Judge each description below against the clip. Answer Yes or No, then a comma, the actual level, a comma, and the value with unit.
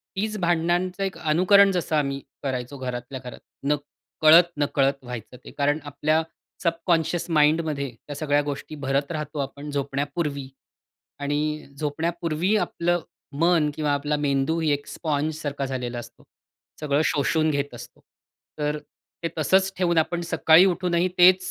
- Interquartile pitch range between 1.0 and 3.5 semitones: Yes, average, 3.2 semitones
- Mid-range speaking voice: Yes, medium, 150 Hz